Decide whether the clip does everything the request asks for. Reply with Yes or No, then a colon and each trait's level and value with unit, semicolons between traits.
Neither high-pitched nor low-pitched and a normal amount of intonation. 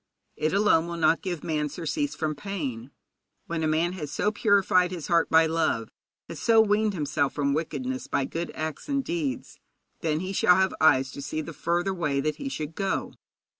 Yes: medium, 165 Hz; average, 4.3 semitones